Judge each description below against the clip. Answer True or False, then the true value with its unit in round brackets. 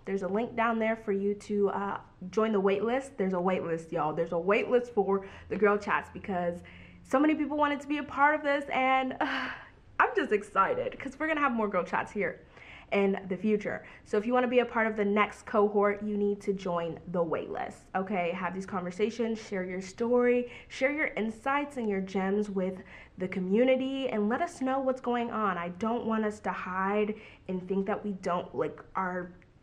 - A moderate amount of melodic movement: True (4.5 semitones)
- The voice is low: False (210 Hz)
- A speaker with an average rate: False (210 wpm)